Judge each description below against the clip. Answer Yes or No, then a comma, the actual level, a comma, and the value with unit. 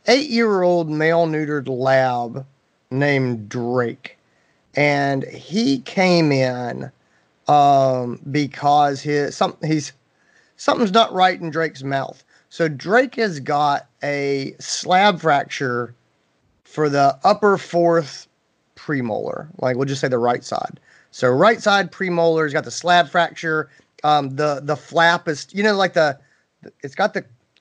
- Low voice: No, medium, 150 Hz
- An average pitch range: Yes, average, 4.2 semitones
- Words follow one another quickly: No, slow, 135 wpm